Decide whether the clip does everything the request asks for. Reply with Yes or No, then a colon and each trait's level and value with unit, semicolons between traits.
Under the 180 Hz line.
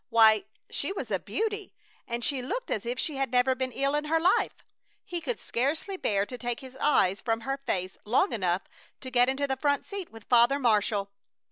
No: very high, 255 Hz